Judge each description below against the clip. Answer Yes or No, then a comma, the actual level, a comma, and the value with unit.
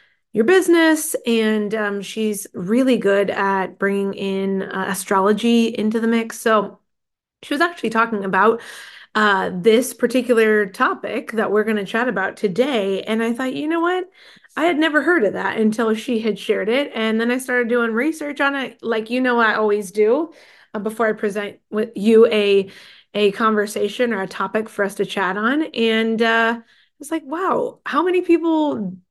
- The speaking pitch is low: No, high, 225 Hz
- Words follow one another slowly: No, average, 185 wpm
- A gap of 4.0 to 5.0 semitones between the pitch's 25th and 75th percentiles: No, average, 3.5 semitones